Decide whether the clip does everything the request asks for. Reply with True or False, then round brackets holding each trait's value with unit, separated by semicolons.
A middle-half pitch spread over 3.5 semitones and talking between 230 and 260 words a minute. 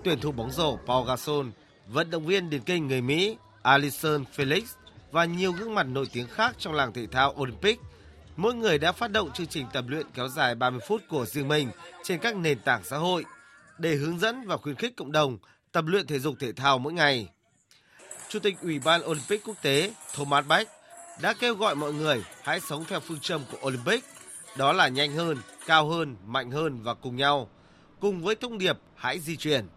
False (4.8 semitones; 210 wpm)